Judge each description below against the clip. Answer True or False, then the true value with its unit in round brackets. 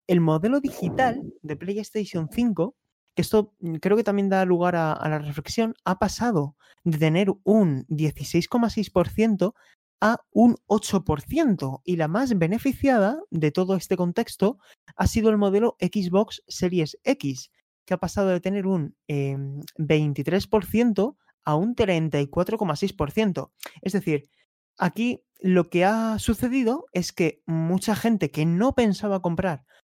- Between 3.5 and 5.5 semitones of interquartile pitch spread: True (5.0 semitones)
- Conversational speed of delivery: True (135 wpm)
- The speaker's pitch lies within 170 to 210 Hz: True (190 Hz)